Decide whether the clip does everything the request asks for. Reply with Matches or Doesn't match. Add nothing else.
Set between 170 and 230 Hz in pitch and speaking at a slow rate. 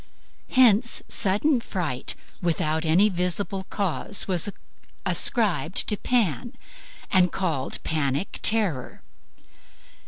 Matches